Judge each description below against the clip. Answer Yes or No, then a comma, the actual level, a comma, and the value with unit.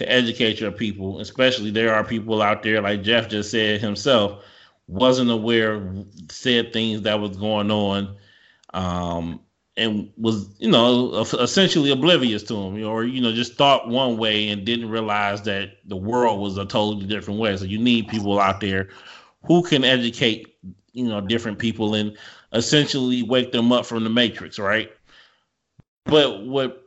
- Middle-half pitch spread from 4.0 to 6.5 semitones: No, average, 2.7 semitones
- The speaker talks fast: No, average, 165 wpm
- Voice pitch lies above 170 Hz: No, low, 110 Hz